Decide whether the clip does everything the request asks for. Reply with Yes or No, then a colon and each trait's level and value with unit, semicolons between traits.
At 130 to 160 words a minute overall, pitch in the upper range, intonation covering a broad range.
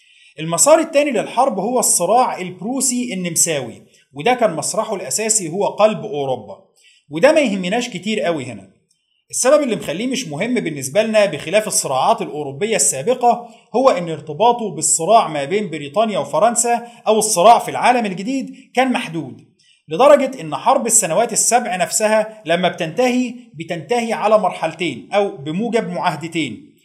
Yes: fast, 135 wpm; high, 215 Hz; wide, 5.9 semitones